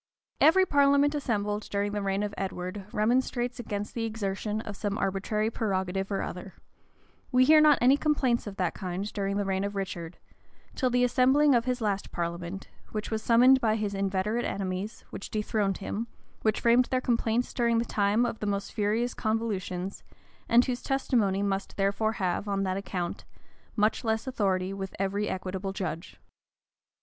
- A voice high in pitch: Yes, high, 210 Hz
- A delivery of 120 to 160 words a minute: No, average, 170 wpm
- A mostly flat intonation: No, average, 3.5 semitones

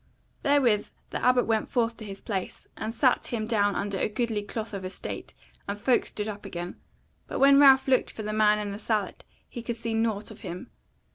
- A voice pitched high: Yes, high, 215 Hz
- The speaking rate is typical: No, fast, 210 wpm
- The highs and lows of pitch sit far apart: No, narrow, 2.6 semitones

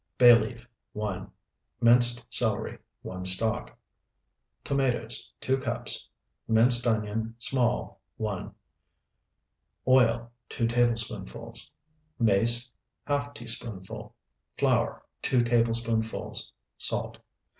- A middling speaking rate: No, slow, 80 wpm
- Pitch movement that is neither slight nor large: No, narrow, 1.5 semitones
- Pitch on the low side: Yes, low, 115 Hz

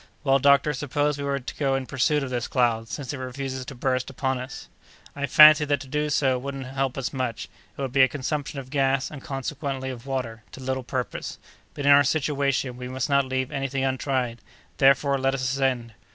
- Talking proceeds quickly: Yes, fast, 210 wpm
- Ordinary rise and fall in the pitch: No, narrow, 1.5 semitones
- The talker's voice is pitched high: No, low, 135 Hz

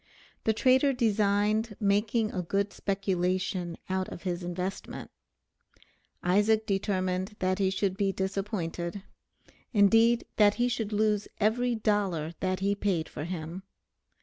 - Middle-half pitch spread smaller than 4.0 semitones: Yes, narrow, 2.5 semitones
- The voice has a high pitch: Yes, high, 200 Hz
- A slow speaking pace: Yes, slow, 125 wpm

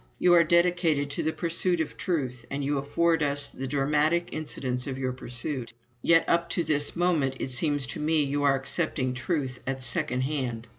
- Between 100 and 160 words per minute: No, average, 190 wpm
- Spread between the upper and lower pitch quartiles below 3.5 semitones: No, average, 3.9 semitones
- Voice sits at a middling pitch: Yes, medium, 145 Hz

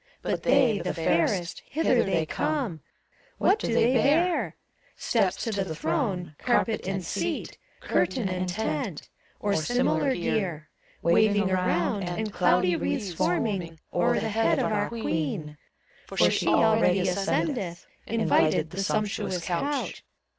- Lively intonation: No, average, 4.4 semitones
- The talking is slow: Yes, slow, 130 wpm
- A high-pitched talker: Yes, high, 195 Hz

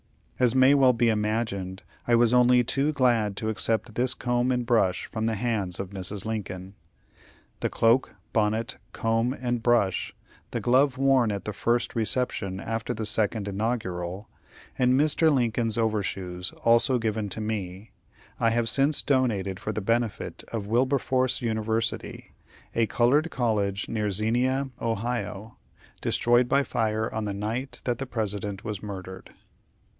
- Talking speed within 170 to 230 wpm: No, average, 150 wpm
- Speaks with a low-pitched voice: Yes, low, 115 Hz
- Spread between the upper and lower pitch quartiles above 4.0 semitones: No, average, 2.9 semitones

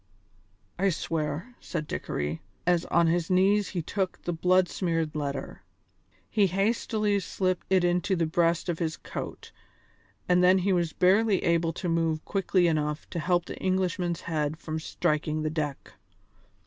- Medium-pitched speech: Yes, medium, 175 Hz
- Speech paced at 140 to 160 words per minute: Yes, average, 155 wpm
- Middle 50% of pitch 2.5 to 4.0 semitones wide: Yes, average, 2.8 semitones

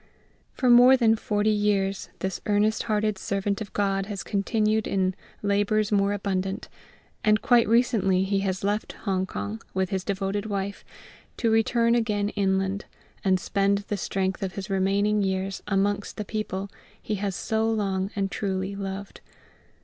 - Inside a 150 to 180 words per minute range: Yes, average, 155 wpm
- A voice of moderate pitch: No, high, 200 Hz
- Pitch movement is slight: Yes, narrow, 1.7 semitones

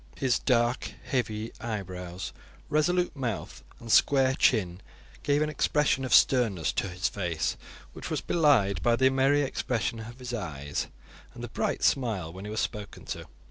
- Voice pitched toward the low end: Yes, low, 115 Hz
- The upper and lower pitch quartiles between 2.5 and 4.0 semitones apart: No, wide, 5.4 semitones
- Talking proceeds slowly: No, average, 160 wpm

